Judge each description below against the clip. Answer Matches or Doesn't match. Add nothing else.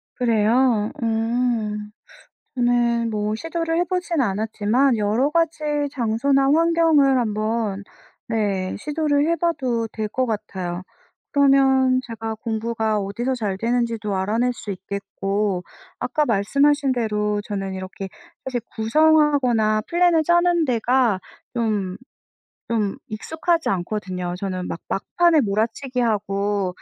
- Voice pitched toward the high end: Matches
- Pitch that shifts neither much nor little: Matches